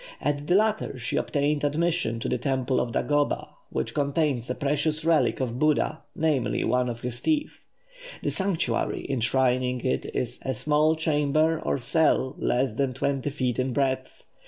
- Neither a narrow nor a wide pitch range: Yes, average, 3.4 semitones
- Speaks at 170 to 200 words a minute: No, average, 160 wpm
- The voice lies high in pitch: No, medium, 140 Hz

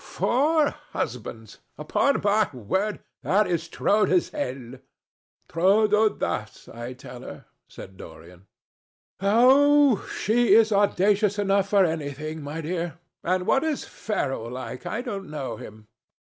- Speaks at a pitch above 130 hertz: Yes, medium, 185 Hz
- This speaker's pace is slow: Yes, slow, 130 wpm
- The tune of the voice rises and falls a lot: Yes, wide, 8.2 semitones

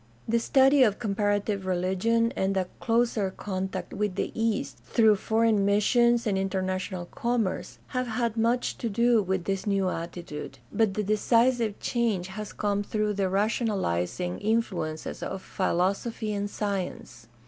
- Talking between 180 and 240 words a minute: No, average, 140 wpm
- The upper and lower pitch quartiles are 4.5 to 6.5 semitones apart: No, average, 3.3 semitones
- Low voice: No, high, 205 Hz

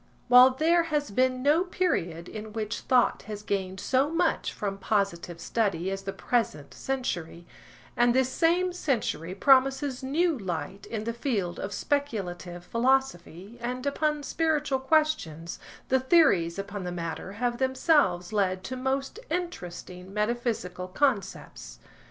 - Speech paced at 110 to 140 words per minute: Yes, slow, 135 wpm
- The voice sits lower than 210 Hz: No, high, 235 Hz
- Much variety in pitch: Yes, wide, 6.4 semitones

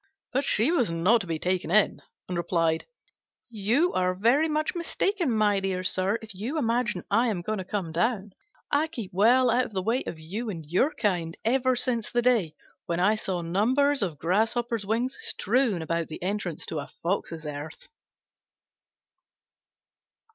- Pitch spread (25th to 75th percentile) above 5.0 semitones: Yes, wide, 5.6 semitones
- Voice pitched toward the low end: No, high, 210 Hz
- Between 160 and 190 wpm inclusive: Yes, average, 170 wpm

